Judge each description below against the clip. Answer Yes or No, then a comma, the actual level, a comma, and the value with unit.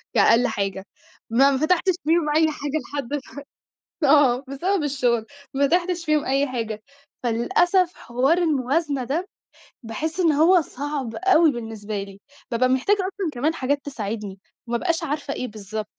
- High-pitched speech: Yes, very high, 280 Hz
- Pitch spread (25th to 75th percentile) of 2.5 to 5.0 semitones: No, wide, 5.4 semitones